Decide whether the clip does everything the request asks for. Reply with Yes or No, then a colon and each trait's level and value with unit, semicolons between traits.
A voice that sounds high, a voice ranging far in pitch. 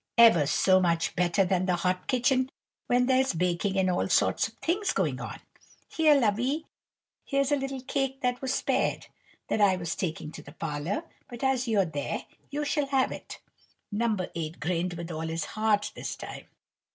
Yes: high, 205 Hz; wide, 7.3 semitones